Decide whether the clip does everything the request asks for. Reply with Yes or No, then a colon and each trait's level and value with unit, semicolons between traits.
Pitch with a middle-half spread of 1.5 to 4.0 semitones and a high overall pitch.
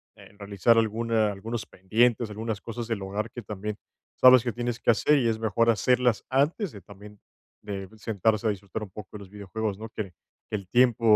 No: narrow, 2.4 semitones; low, 110 Hz